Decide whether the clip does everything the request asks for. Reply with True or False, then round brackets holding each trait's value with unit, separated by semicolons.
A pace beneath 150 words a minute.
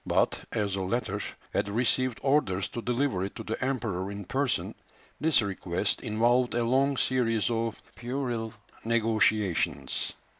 True (140 wpm)